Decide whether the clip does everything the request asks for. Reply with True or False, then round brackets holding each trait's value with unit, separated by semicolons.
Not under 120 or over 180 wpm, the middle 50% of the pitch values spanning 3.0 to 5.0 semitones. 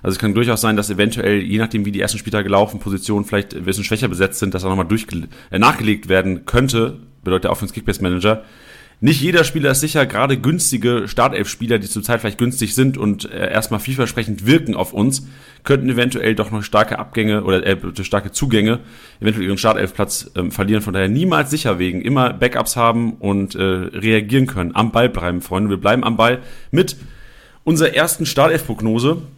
False (190 wpm; 3.7 semitones)